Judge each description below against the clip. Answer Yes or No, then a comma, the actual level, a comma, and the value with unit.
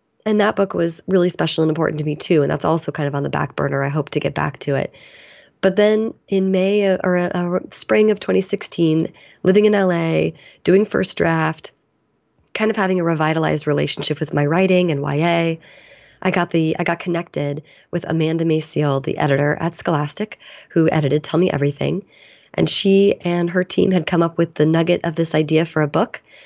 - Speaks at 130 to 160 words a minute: No, average, 200 wpm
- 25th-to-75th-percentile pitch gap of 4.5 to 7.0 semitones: No, average, 3.3 semitones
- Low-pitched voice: No, medium, 170 Hz